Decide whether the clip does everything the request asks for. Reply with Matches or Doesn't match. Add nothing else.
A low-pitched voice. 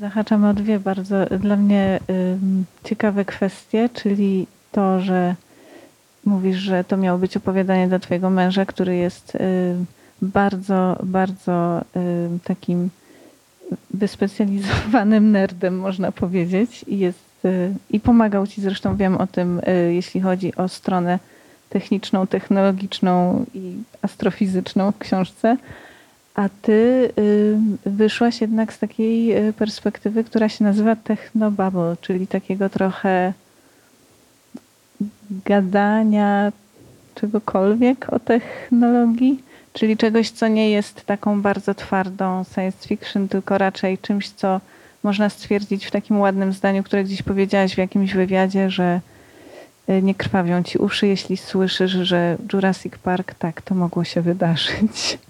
Doesn't match